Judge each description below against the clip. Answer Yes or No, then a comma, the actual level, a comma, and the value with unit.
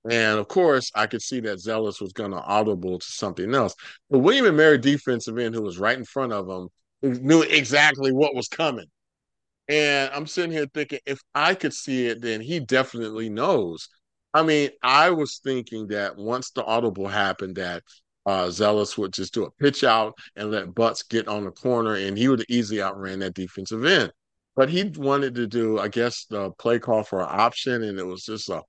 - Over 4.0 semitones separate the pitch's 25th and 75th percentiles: Yes, average, 4.7 semitones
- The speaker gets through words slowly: No, fast, 205 wpm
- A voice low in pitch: Yes, low, 115 Hz